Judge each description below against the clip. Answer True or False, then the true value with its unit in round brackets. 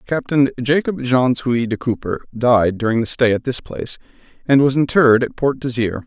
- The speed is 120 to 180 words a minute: False (190 wpm)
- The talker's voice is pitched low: True (125 Hz)